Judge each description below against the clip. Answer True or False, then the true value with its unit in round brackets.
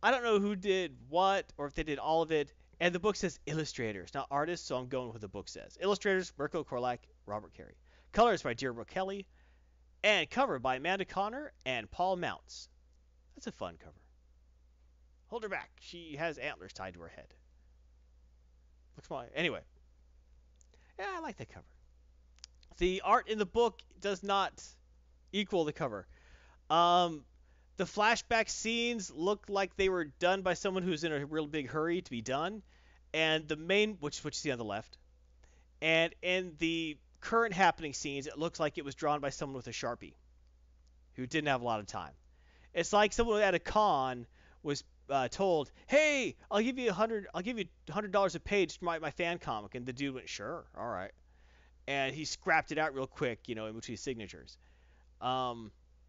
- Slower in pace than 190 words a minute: False (195 wpm)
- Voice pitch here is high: False (140 Hz)